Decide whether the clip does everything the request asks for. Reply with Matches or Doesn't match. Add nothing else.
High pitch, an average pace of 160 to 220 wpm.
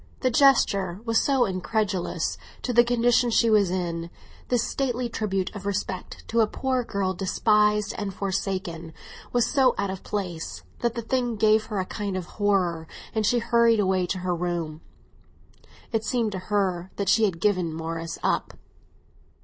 Matches